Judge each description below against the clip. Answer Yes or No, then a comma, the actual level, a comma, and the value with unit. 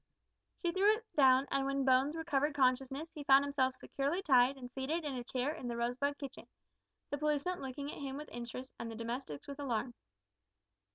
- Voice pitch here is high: Yes, very high, 275 Hz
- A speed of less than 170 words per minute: No, average, 190 wpm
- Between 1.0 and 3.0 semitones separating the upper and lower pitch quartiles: Yes, narrow, 2.4 semitones